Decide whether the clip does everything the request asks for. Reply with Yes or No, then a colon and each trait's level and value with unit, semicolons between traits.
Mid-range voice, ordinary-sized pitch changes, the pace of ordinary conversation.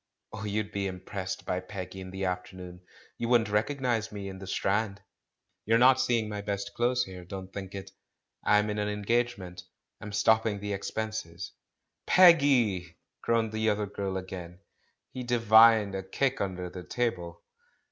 No: low, 105 Hz; average, 3.0 semitones; average, 165 wpm